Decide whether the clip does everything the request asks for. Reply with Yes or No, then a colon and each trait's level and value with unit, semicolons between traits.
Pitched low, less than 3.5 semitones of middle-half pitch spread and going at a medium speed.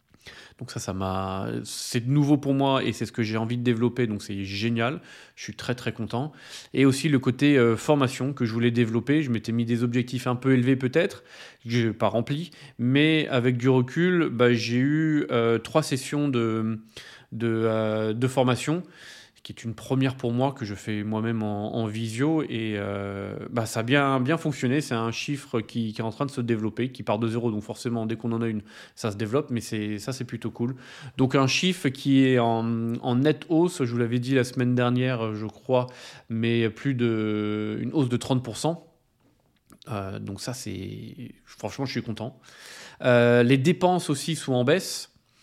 Yes: low, 120 Hz; average, 3.0 semitones; average, 205 wpm